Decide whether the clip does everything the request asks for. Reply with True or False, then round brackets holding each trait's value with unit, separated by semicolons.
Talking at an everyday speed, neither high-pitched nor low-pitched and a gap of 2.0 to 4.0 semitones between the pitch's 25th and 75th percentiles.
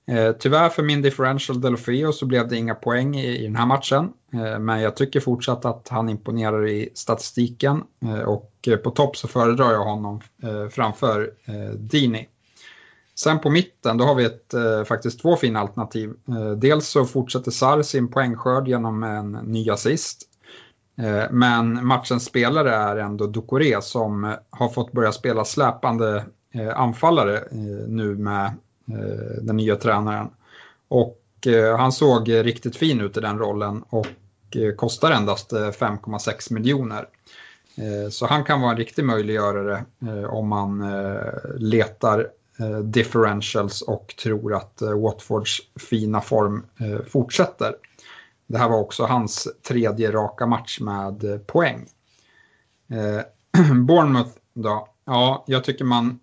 False (140 wpm; 115 Hz; 2.8 semitones)